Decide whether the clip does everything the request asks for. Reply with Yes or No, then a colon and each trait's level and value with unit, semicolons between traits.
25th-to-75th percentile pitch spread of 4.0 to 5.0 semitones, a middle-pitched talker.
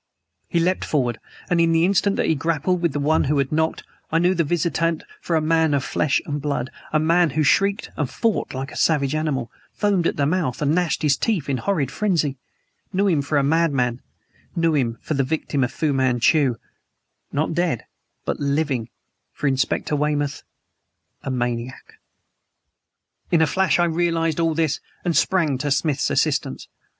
No: average, 3.3 semitones; medium, 155 Hz